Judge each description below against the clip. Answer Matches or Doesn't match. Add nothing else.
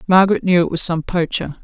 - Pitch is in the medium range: Matches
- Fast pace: Matches